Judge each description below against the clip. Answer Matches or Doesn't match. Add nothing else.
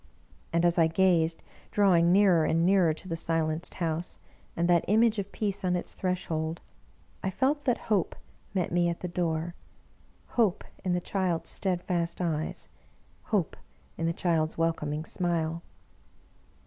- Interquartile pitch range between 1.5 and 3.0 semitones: Matches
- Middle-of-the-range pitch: Matches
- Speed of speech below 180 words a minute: Matches